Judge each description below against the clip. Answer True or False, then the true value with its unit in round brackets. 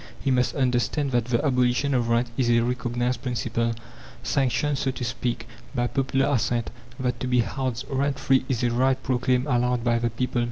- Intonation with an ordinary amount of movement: False (1.7 semitones)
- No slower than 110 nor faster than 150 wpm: False (190 wpm)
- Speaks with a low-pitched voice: True (125 Hz)